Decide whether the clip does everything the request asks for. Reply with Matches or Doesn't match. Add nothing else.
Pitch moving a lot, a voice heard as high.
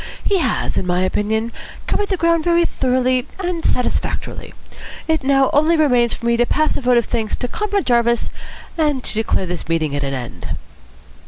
Matches